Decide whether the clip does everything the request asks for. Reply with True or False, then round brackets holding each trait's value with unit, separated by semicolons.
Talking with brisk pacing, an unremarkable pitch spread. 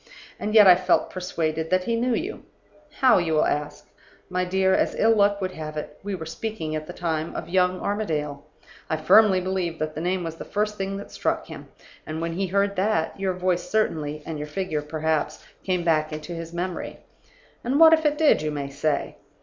True (210 wpm; 4.2 semitones)